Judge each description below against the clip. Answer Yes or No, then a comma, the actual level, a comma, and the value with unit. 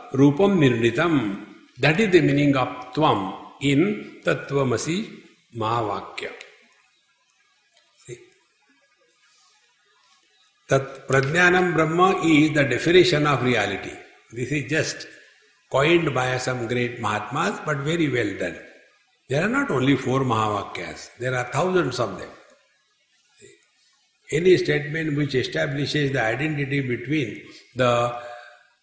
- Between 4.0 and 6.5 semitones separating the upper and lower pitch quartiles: Yes, average, 4.4 semitones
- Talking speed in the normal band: No, slow, 85 wpm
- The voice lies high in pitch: No, medium, 140 Hz